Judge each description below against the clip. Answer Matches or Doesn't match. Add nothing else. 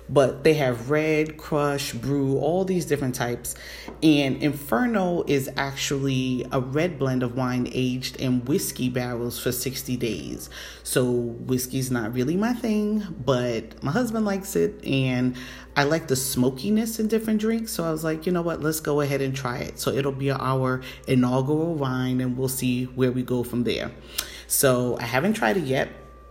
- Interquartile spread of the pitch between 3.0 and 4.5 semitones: Matches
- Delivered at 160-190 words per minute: Matches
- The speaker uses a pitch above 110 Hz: Matches